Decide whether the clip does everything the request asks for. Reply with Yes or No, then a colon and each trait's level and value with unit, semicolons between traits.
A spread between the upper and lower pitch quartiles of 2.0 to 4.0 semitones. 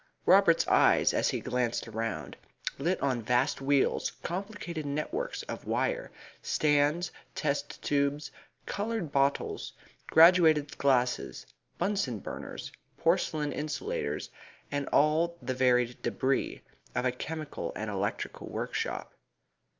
No: average, 4.9 semitones